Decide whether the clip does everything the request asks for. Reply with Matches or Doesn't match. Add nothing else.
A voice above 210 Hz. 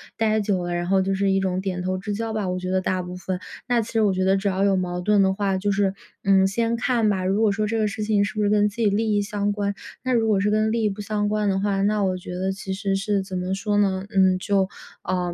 Doesn't match